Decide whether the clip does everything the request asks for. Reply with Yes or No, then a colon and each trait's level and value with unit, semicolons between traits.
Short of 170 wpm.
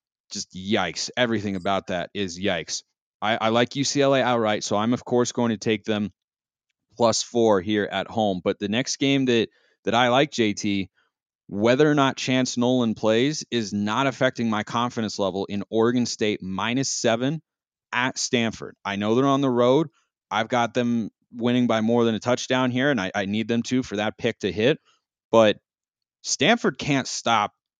No: average, 180 wpm